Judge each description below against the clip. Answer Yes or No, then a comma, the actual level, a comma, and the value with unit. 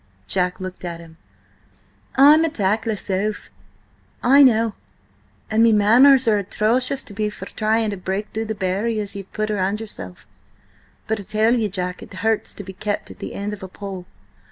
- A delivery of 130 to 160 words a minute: No, average, 195 wpm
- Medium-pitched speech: No, high, 210 Hz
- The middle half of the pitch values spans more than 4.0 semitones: No, average, 2.8 semitones